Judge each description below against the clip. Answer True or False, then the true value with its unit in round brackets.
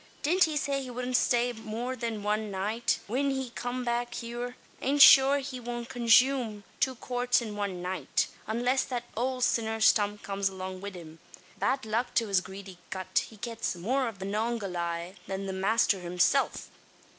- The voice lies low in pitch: False (230 Hz)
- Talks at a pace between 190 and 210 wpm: False (175 wpm)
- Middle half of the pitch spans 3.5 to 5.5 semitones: True (4.1 semitones)